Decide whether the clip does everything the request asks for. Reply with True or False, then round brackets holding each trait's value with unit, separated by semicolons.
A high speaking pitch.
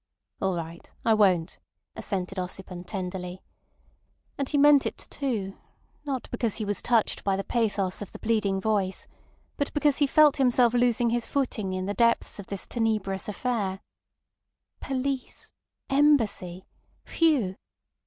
True (215 Hz)